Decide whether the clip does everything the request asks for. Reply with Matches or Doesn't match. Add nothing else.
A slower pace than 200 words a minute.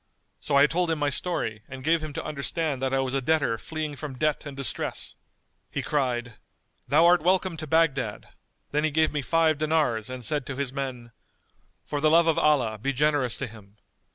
Doesn't match